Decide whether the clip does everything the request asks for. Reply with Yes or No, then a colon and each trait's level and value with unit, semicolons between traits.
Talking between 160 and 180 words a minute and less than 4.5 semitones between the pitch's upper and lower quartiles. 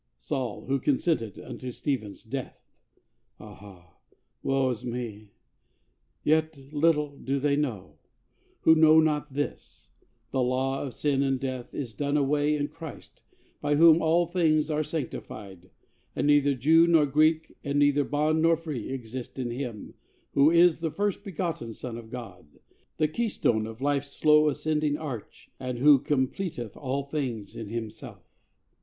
No: average, 150 wpm; average, 4.0 semitones